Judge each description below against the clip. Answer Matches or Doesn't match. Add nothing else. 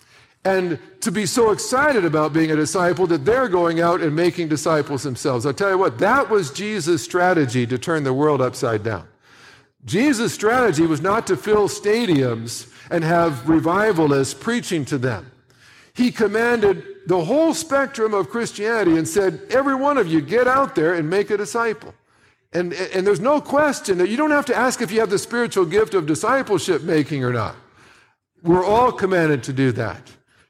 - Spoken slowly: Doesn't match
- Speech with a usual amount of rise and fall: Doesn't match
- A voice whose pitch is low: Doesn't match